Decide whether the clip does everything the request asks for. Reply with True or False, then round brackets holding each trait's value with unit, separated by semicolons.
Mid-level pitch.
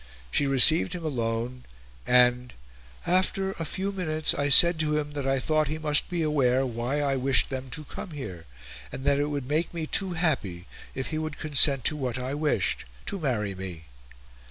True (145 Hz)